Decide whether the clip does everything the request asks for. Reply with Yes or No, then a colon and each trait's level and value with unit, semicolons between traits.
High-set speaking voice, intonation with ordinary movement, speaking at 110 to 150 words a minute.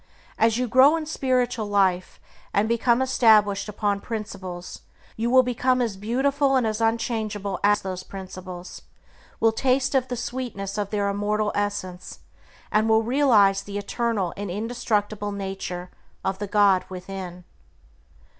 Yes: high, 210 Hz; average, 3.4 semitones; average, 140 wpm